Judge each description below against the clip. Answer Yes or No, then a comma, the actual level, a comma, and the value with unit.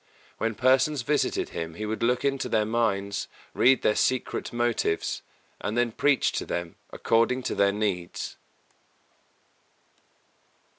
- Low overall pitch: Yes, low, 115 Hz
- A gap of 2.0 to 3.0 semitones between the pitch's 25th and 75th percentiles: No, average, 3.8 semitones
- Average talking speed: No, slow, 130 wpm